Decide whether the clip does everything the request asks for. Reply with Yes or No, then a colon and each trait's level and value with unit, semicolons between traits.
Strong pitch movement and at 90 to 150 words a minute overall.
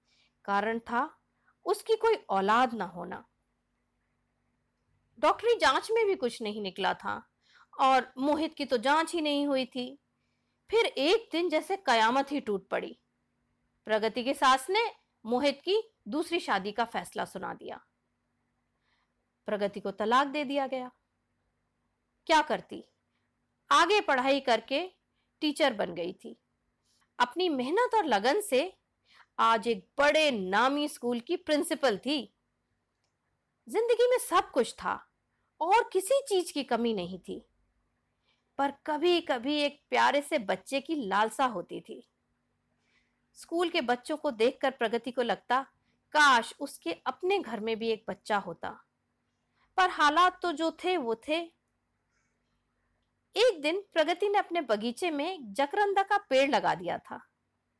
Yes: wide, 6.8 semitones; average, 135 wpm